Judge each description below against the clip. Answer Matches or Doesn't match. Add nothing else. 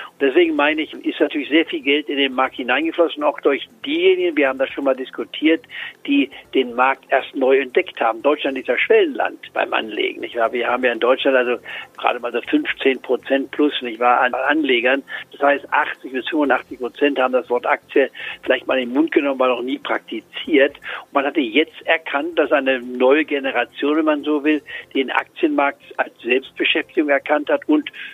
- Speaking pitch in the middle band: Matches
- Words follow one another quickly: Matches